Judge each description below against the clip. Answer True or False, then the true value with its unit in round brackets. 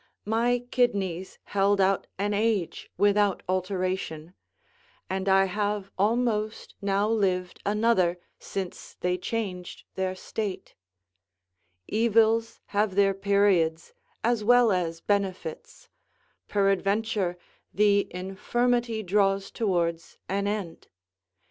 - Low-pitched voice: False (200 Hz)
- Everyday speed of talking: False (100 wpm)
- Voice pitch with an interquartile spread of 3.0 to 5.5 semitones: False (2.6 semitones)